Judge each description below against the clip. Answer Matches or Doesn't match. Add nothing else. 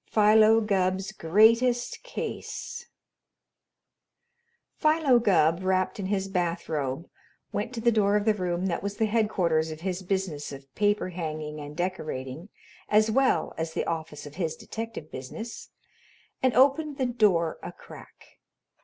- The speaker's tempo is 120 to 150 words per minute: Matches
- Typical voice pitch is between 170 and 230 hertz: Matches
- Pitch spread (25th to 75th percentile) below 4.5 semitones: Doesn't match